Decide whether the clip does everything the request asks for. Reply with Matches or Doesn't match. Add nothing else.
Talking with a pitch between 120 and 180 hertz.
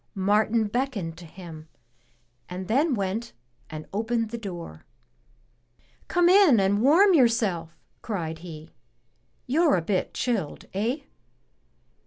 Doesn't match